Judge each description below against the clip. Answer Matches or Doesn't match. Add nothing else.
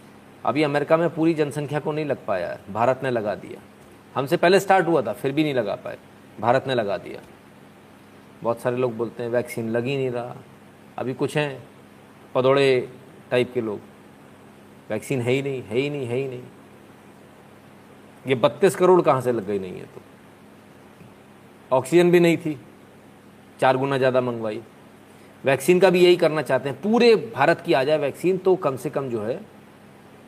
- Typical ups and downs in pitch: Doesn't match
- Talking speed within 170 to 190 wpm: Matches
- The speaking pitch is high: Doesn't match